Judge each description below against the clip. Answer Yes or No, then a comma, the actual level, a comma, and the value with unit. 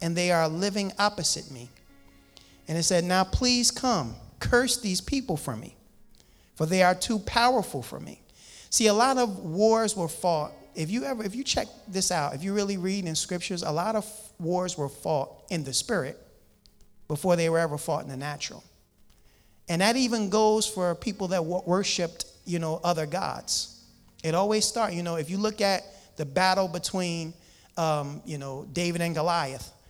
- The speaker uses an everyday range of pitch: Yes, average, 5.0 semitones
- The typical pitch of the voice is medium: Yes, medium, 175 Hz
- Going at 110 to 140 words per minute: No, average, 185 wpm